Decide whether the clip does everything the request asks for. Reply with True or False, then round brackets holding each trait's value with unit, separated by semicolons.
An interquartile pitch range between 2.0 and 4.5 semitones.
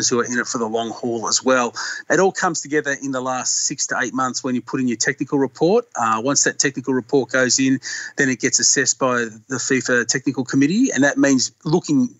True (2.9 semitones)